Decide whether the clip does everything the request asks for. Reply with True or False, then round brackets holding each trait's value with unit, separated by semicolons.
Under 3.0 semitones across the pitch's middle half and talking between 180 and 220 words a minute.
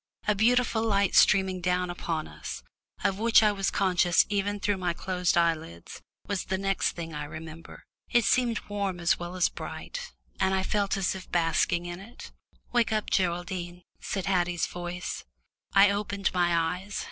False (2.6 semitones; 170 wpm)